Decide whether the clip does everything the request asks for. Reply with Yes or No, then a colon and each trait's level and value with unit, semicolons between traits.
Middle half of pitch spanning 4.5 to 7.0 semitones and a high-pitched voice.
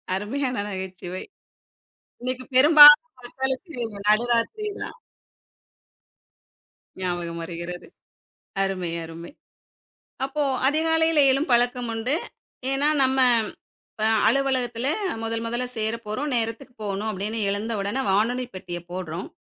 Yes: wide, 5.5 semitones; high, 230 Hz